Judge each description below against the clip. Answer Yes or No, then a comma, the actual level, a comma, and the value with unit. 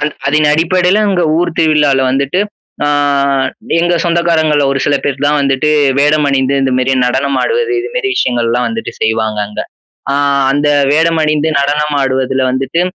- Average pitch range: Yes, average, 3.5 semitones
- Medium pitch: Yes, medium, 145 Hz